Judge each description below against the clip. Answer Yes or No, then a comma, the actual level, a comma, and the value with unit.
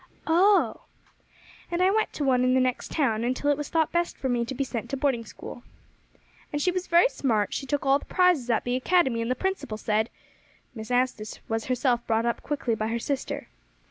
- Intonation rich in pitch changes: No, average, 4.4 semitones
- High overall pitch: Yes, very high, 260 Hz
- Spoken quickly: Yes, fast, 220 wpm